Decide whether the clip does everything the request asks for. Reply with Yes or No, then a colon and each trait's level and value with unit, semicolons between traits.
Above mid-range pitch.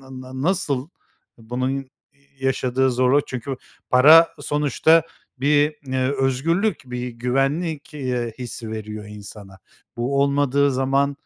No: low, 135 Hz